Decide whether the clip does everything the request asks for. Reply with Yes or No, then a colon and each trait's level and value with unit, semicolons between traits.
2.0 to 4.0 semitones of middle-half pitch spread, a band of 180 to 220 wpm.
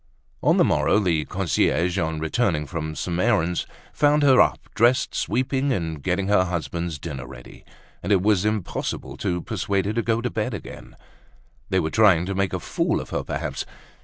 No: average, 4.8 semitones; average, 185 wpm